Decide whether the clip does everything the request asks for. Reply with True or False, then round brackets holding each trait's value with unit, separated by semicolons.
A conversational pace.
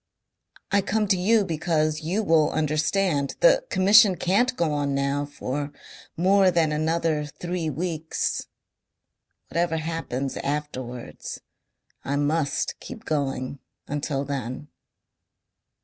False (110 wpm)